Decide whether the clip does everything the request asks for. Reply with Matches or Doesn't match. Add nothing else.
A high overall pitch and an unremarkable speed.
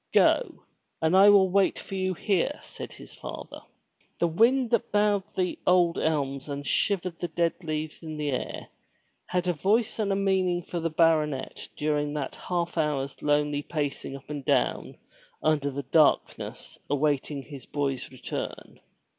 Doesn't match